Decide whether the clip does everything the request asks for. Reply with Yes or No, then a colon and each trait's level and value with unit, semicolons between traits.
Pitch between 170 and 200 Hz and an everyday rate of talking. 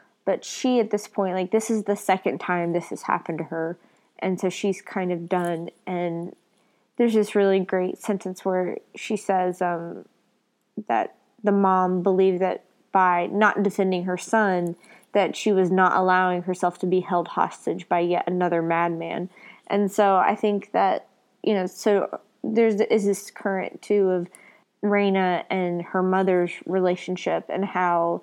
Yes: medium, 185 Hz; average, 165 wpm